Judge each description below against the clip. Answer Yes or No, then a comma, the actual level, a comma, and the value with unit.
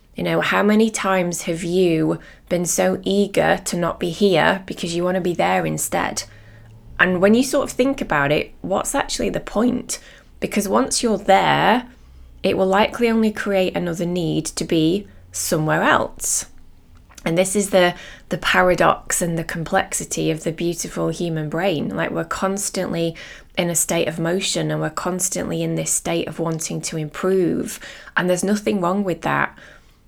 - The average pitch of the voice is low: No, medium, 175 Hz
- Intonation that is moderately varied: Yes, average, 3.6 semitones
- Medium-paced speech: Yes, average, 170 wpm